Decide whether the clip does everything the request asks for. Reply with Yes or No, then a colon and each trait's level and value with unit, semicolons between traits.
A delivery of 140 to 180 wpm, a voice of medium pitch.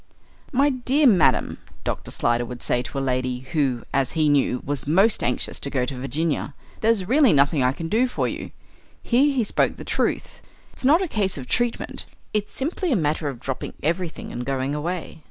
No: average, 195 wpm; medium, 155 Hz